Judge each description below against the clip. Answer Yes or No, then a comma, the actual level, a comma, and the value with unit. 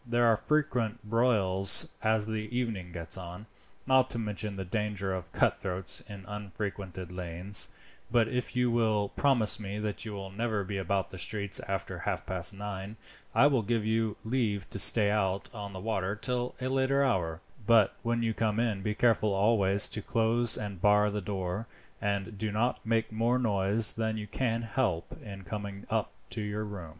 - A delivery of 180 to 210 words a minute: Yes, average, 185 wpm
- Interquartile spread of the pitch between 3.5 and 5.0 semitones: No, average, 2.8 semitones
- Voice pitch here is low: Yes, low, 105 Hz